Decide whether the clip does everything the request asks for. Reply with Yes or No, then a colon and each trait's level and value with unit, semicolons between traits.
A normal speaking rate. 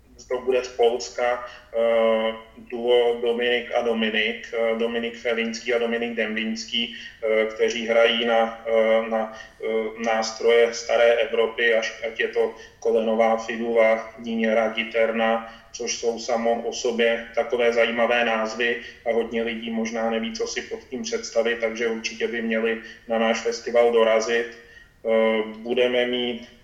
Yes: average, 140 wpm